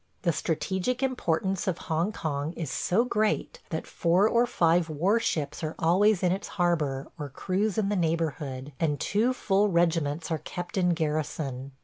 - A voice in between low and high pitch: Yes, medium, 170 Hz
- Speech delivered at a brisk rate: No, average, 165 wpm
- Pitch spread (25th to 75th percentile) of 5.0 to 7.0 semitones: No, average, 4.0 semitones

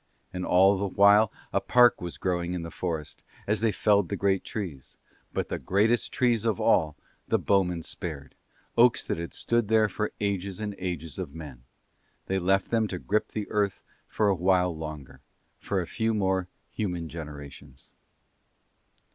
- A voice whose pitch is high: No, very low, 95 Hz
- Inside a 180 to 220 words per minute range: No, average, 170 wpm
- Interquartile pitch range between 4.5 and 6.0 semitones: No, average, 4.0 semitones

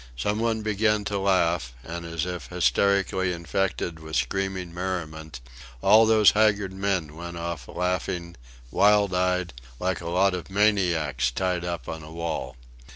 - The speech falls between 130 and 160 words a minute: Yes, average, 150 wpm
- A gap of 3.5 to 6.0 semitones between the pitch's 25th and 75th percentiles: No, average, 2.9 semitones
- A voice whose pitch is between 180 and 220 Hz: No, very low, 90 Hz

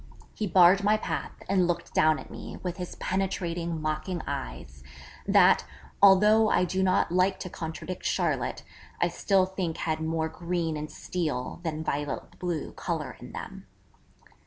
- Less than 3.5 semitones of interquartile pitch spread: Yes, average, 2.9 semitones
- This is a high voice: No, medium, 175 Hz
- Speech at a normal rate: Yes, average, 155 wpm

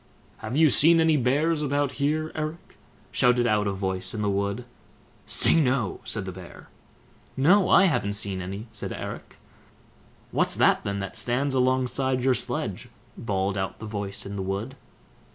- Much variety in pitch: Yes, wide, 6.0 semitones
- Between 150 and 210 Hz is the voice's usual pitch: No, low, 120 Hz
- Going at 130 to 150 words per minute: No, average, 165 wpm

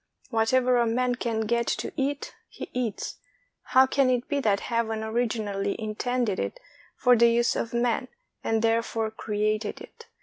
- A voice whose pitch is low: No, high, 230 Hz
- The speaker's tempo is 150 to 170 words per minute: Yes, average, 165 wpm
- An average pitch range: No, narrow, 2.1 semitones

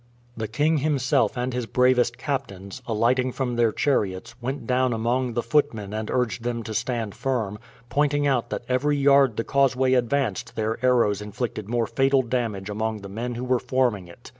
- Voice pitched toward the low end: Yes, low, 120 Hz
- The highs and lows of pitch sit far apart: No, average, 2.9 semitones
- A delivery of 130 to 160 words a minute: No, average, 180 wpm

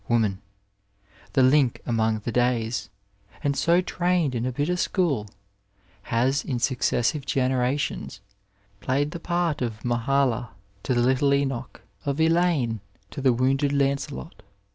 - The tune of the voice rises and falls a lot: No, average, 3.4 semitones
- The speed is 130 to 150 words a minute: Yes, slow, 135 wpm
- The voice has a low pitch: Yes, low, 130 Hz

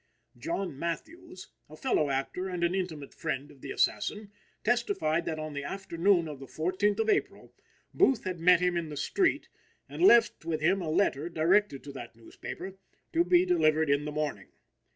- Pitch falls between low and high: Yes, medium, 170 Hz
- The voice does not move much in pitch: No, average, 4.9 semitones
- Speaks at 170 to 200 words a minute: Yes, average, 180 wpm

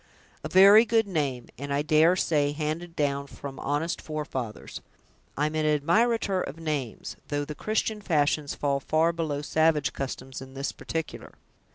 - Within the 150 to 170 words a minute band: Yes, average, 155 wpm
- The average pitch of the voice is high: No, medium, 150 Hz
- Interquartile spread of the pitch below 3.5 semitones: Yes, average, 2.9 semitones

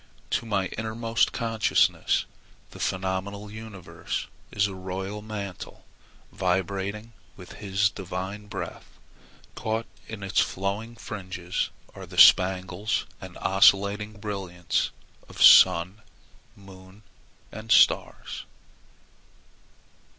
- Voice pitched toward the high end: No, low, 100 Hz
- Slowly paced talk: Yes, slow, 95 wpm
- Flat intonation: Yes, narrow, 2.3 semitones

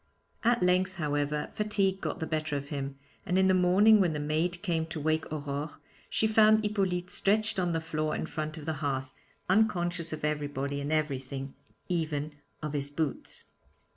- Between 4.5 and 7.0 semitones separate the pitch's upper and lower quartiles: No, average, 3.9 semitones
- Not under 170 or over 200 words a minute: Yes, average, 175 wpm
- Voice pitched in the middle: Yes, medium, 160 Hz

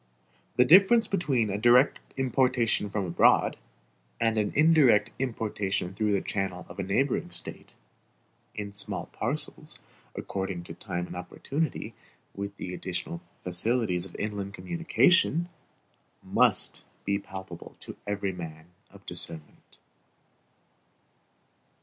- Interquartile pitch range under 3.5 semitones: No, wide, 5.4 semitones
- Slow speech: Yes, slow, 115 wpm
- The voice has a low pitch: Yes, low, 105 Hz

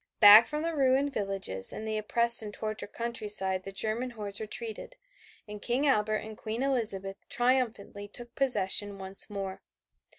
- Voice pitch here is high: Yes, high, 215 Hz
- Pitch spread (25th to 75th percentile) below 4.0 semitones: Yes, average, 3.1 semitones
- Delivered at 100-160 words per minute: Yes, average, 155 wpm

